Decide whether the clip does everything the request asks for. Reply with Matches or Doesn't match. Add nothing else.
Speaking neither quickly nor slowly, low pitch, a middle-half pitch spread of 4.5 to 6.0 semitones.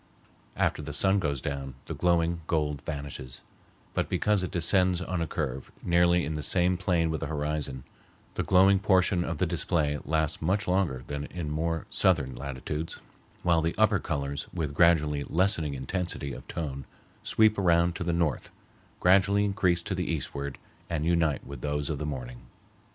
Doesn't match